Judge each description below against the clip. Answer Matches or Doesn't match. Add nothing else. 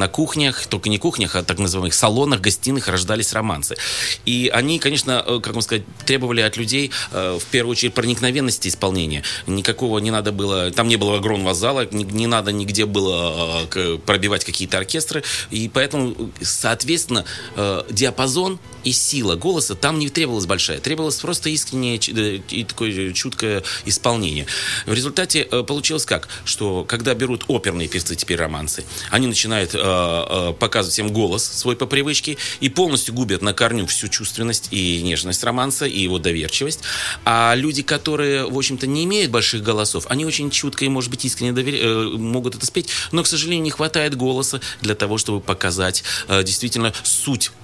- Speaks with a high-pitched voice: Doesn't match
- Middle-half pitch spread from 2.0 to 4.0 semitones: Doesn't match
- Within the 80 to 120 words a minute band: Doesn't match